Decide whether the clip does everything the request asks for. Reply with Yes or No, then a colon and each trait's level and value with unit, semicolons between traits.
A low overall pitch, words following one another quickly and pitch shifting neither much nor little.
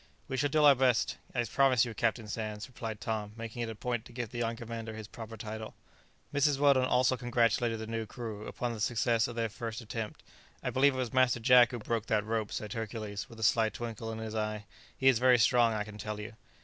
No: low, 115 Hz; fast, 235 wpm; narrow, 2.0 semitones